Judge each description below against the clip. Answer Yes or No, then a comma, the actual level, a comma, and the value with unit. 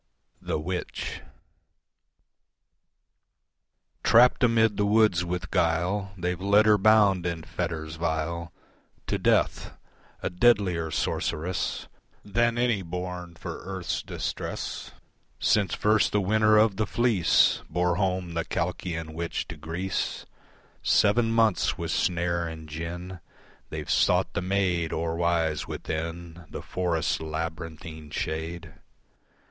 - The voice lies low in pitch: Yes, very low, 90 Hz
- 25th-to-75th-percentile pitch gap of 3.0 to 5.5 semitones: Yes, average, 3.6 semitones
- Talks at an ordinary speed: No, slow, 115 wpm